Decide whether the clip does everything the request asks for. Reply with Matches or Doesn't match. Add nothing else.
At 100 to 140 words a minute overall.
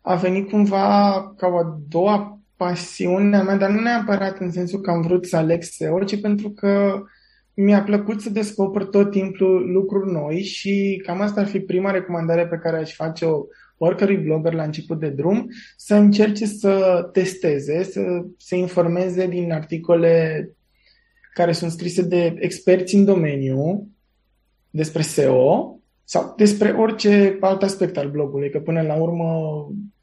Doesn't match